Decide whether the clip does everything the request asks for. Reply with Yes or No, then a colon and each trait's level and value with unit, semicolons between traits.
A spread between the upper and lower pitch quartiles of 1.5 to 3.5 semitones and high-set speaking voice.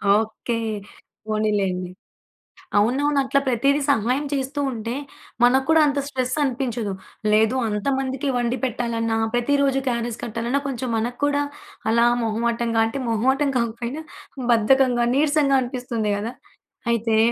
Yes: average, 3.0 semitones; high, 240 Hz